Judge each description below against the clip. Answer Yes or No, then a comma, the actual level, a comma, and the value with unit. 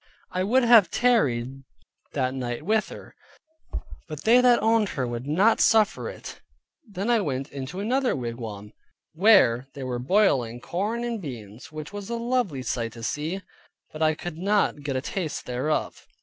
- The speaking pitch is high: No, medium, 155 Hz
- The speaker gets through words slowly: No, average, 165 wpm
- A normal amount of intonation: No, wide, 8.9 semitones